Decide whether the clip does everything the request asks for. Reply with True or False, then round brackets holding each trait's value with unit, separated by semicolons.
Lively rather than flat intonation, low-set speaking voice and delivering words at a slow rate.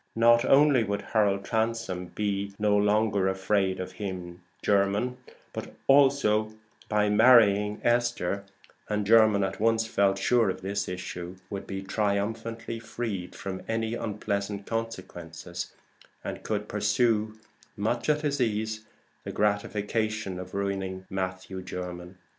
False (2.6 semitones; 105 Hz; 125 wpm)